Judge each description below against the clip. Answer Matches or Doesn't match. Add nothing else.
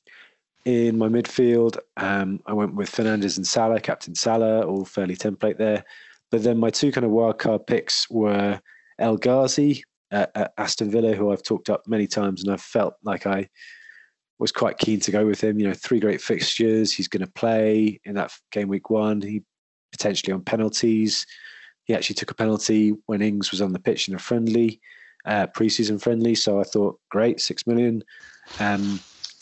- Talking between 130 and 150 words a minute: Doesn't match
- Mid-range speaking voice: Doesn't match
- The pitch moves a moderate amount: Doesn't match